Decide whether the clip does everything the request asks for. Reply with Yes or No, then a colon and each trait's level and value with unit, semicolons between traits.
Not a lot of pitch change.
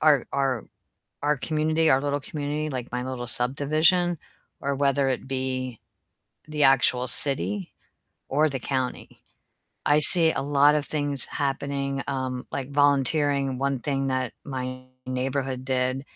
Yes: narrow, 2.1 semitones